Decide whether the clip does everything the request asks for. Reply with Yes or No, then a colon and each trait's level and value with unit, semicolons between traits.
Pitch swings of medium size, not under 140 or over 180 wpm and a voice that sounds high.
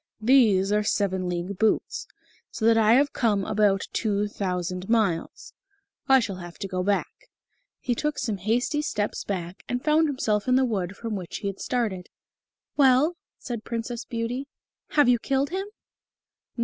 Yes: average, 4.5 semitones; average, 160 wpm; high, 220 Hz